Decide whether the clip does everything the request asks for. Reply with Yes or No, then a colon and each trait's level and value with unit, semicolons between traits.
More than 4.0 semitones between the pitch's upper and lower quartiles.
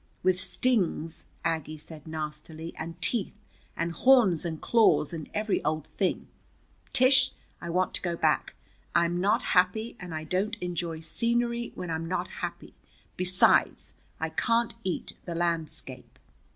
Yes: average, 5.0 semitones